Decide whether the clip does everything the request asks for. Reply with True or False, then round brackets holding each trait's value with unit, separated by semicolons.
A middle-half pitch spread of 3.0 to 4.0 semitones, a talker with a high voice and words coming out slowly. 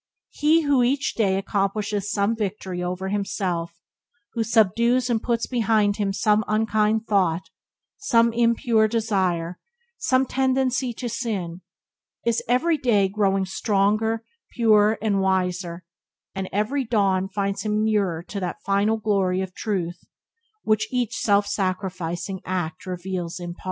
True (3.3 semitones; 205 Hz; 130 wpm)